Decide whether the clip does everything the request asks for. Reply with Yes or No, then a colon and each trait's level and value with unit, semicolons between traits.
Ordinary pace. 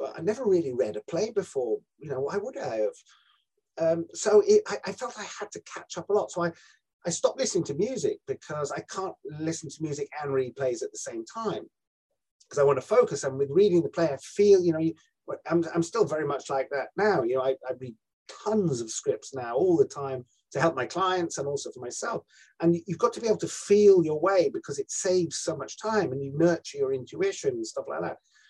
No: fast, 240 wpm